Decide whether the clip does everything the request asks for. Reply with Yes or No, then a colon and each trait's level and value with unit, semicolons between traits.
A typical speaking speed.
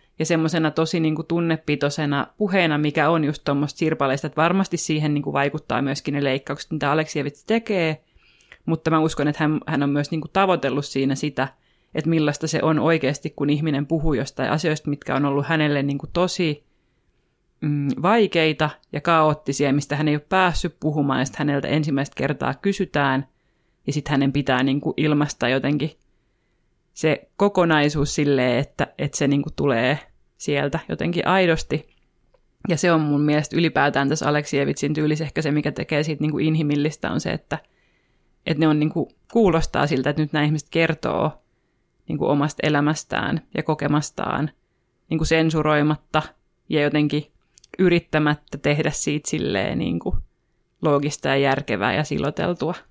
No: fast, 160 wpm